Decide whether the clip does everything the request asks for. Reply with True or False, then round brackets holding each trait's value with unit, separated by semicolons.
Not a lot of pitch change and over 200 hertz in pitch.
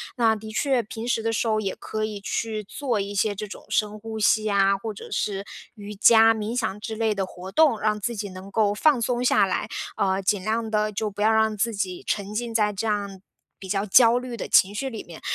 True (2.0 semitones; 215 Hz)